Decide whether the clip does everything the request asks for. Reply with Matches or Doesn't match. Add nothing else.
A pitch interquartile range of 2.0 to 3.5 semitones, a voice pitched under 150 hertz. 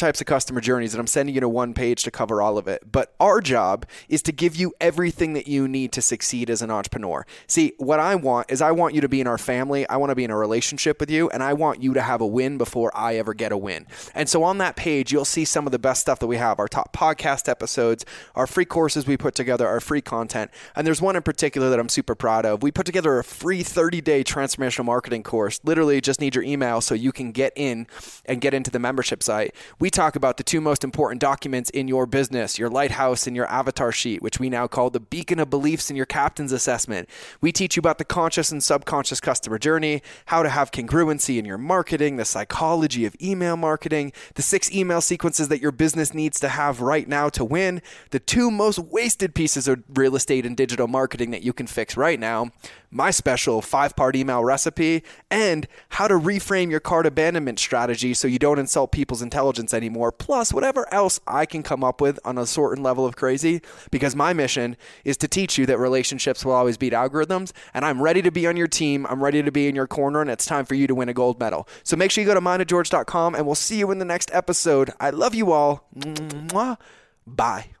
Doesn't match